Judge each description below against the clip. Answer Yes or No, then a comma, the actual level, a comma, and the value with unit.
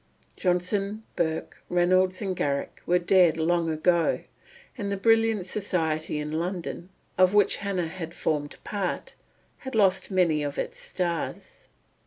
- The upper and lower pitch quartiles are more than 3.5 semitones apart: No, average, 3.1 semitones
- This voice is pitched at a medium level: Yes, medium, 180 Hz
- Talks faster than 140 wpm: No, slow, 135 wpm